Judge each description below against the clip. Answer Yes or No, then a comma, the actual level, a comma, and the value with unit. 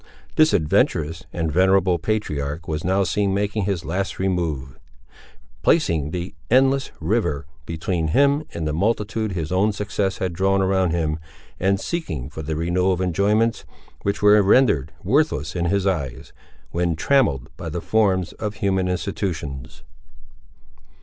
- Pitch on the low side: Yes, very low, 95 Hz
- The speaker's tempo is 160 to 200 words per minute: No, average, 145 wpm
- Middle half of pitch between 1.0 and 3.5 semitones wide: No, average, 4.2 semitones